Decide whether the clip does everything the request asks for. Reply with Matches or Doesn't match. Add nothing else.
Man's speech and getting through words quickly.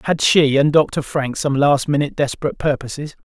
Doesn't match